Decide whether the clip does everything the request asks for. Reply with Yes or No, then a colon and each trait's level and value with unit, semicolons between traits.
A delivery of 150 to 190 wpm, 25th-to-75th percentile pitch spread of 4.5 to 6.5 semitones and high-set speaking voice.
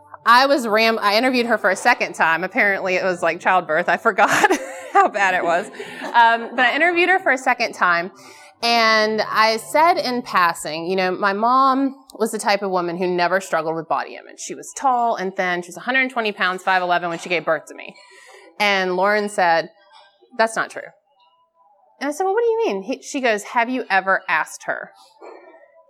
No: average, 200 wpm; wide, 5.6 semitones; high, 215 Hz